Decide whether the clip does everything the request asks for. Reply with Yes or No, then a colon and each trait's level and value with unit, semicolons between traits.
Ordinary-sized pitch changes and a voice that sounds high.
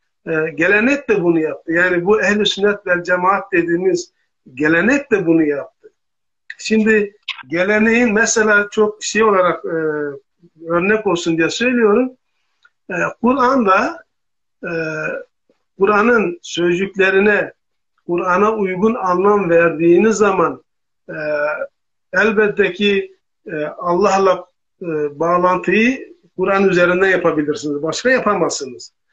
Yes: average, 4.1 semitones; high, 195 Hz